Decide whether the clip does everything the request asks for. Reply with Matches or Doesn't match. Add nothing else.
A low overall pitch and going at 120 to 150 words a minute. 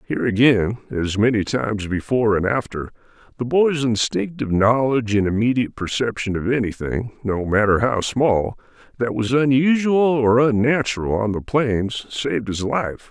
Matches